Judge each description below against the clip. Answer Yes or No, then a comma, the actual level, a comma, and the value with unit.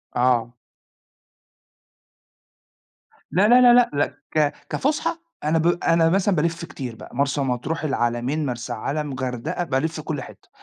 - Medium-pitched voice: Yes, medium, 150 Hz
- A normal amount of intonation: Yes, average, 4.7 semitones